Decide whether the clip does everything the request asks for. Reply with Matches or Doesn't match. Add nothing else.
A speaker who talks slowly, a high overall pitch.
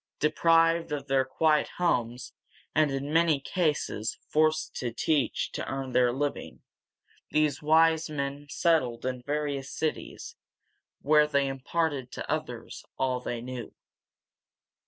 Doesn't match